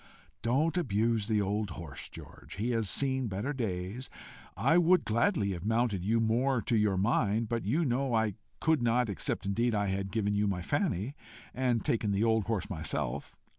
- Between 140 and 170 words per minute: No, average, 180 wpm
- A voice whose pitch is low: Yes, low, 110 Hz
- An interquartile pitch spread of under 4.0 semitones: Yes, average, 3.6 semitones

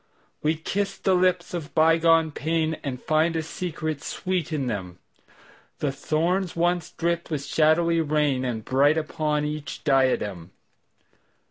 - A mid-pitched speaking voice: Yes, medium, 155 Hz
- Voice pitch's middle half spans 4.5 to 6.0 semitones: No, average, 2.8 semitones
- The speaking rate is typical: No, slow, 120 wpm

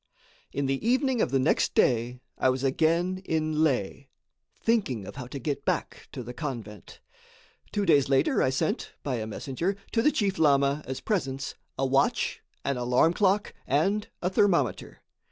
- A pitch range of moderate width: No, wide, 6.1 semitones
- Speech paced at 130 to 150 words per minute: No, average, 170 wpm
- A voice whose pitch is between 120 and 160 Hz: Yes, medium, 140 Hz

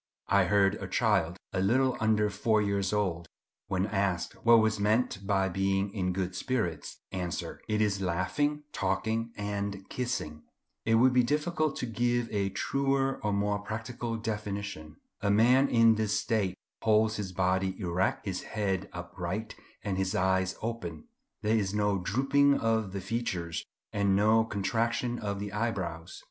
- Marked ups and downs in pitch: No, average, 3.0 semitones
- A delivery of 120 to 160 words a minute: Yes, average, 155 wpm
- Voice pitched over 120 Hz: No, low, 105 Hz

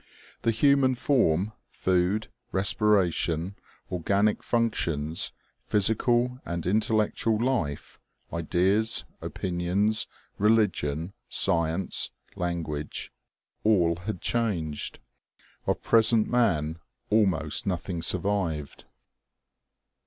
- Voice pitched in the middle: No, very low, 95 Hz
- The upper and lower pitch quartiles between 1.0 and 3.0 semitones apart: No, average, 4.7 semitones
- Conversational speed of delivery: No, slow, 75 wpm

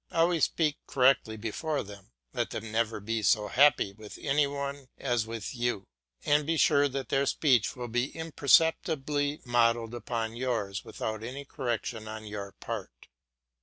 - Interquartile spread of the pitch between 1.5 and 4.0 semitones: No, average, 4.4 semitones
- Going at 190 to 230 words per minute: No, average, 155 wpm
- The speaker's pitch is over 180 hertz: No, low, 120 Hz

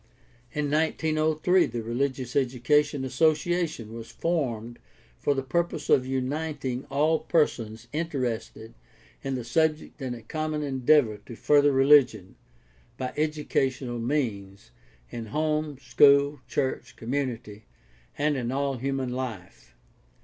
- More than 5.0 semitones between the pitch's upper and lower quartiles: No, average, 3.9 semitones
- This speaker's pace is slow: Yes, slow, 115 wpm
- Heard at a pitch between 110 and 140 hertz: Yes, low, 135 Hz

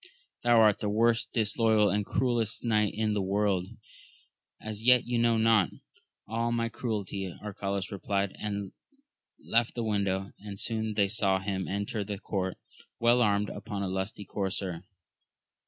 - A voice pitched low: Yes, low, 105 Hz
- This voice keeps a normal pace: Yes, average, 150 wpm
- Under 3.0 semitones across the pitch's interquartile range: Yes, narrow, 2.4 semitones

